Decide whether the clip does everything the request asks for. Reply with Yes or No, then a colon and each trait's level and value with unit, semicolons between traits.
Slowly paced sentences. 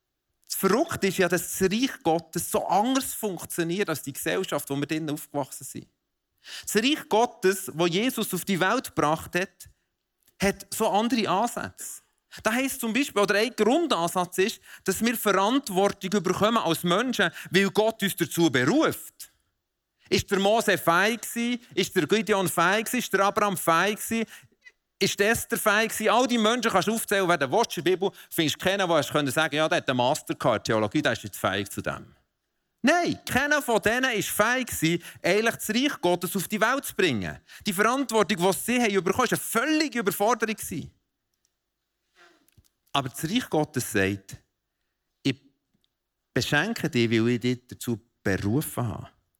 No: average, 165 wpm